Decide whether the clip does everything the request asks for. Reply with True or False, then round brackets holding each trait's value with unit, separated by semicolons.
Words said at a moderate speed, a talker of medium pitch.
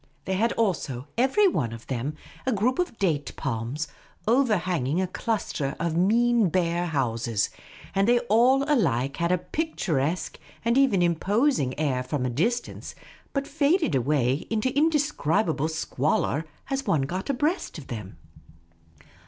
True (145 wpm; 180 Hz)